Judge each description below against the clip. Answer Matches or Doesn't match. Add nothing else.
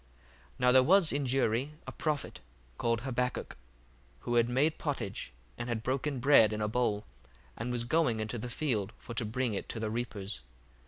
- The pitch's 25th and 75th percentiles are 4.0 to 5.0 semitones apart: Doesn't match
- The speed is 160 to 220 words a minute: Matches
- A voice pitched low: Matches